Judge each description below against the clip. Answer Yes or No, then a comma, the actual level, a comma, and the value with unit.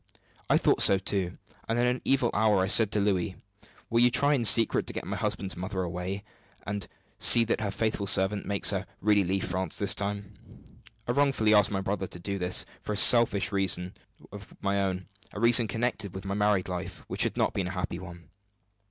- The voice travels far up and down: No, narrow, 2.5 semitones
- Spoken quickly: Yes, fast, 210 wpm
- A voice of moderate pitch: No, low, 100 Hz